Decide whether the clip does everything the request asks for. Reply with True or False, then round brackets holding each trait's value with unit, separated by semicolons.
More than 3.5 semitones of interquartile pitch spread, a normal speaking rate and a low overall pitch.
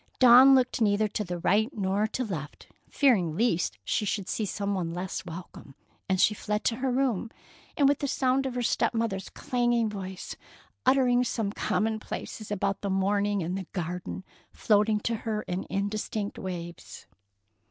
False (3.9 semitones; 165 wpm; 210 Hz)